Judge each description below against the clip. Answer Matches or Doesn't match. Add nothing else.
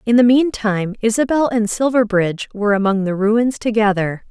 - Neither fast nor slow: Matches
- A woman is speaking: Matches